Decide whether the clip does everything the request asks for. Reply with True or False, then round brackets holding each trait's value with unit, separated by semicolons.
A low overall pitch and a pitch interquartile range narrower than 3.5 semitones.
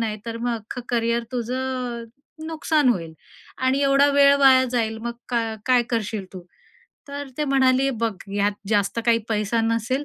False (240 Hz; 2.9 semitones)